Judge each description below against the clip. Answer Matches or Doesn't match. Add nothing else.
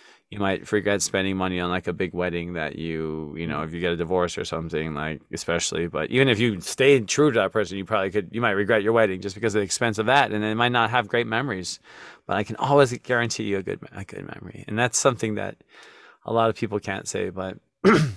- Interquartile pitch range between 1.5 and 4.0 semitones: Doesn't match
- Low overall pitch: Matches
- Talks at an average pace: Doesn't match